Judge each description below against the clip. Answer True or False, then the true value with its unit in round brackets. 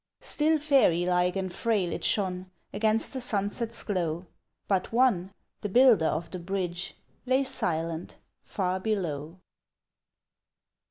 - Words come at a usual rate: False (120 wpm)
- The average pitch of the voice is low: False (190 Hz)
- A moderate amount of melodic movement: True (4.4 semitones)